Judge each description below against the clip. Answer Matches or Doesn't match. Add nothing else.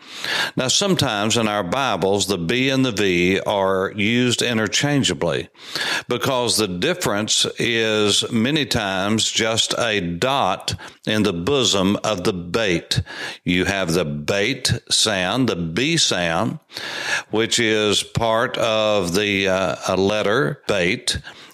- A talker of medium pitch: Doesn't match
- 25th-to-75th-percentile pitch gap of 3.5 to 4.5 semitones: Matches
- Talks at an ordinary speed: Doesn't match